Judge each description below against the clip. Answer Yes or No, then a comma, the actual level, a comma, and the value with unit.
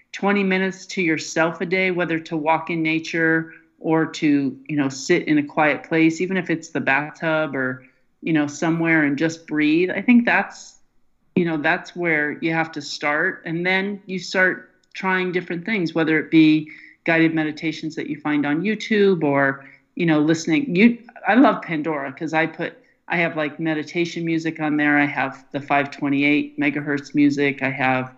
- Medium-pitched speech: Yes, medium, 160 Hz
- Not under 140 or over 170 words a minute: No, average, 185 wpm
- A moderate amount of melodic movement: Yes, average, 3.1 semitones